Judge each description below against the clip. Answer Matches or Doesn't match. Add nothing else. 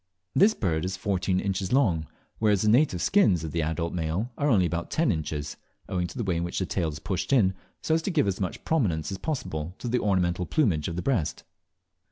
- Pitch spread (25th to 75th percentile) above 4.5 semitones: Matches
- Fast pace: Matches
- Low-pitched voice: Matches